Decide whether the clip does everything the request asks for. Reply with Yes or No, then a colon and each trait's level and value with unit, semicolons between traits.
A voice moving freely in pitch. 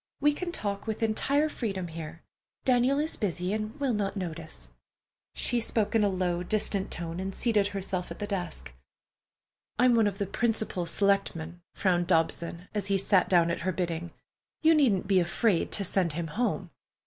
No: average, 4.2 semitones